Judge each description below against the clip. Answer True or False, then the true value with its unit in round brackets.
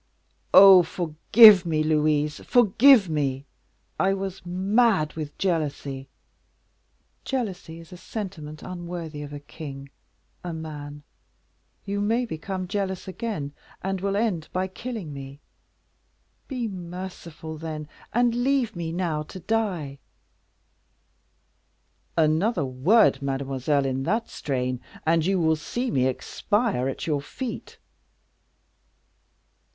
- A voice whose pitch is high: False (170 Hz)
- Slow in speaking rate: True (115 wpm)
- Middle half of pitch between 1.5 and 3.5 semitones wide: False (5.0 semitones)